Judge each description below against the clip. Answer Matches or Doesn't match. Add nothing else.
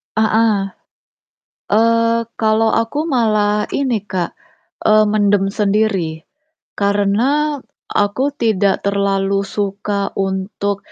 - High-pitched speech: Matches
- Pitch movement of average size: Doesn't match